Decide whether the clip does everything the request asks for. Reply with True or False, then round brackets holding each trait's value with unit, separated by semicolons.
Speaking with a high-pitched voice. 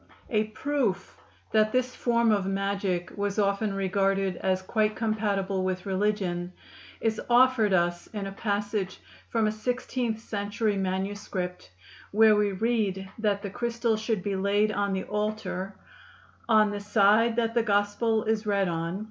True (205 Hz)